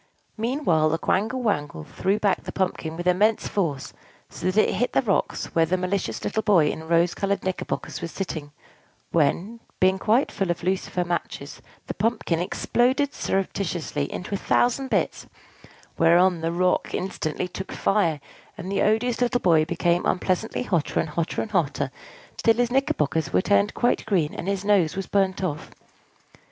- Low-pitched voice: No, medium, 185 Hz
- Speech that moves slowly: No, average, 165 wpm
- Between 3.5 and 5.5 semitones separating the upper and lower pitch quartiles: Yes, average, 4.2 semitones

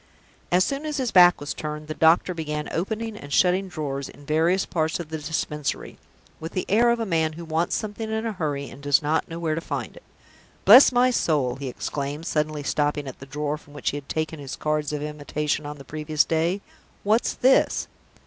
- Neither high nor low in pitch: Yes, medium, 155 Hz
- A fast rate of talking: Yes, fast, 215 wpm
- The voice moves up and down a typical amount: Yes, average, 3.8 semitones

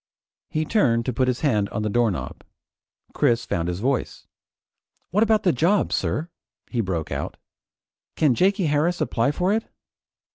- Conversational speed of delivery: Yes, average, 155 wpm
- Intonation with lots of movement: Yes, wide, 7.3 semitones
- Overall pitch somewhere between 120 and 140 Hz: Yes, low, 135 Hz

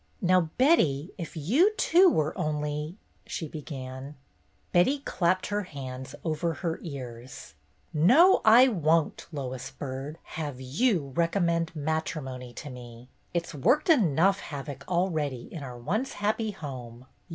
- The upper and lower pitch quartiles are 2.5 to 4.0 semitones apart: No, average, 5.3 semitones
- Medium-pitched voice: Yes, medium, 155 Hz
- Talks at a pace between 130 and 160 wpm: Yes, average, 145 wpm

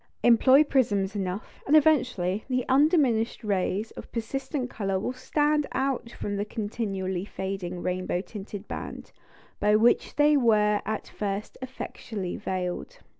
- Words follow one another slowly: Yes, slow, 130 wpm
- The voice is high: Yes, high, 215 Hz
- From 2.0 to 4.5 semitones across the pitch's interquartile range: No, average, 4.9 semitones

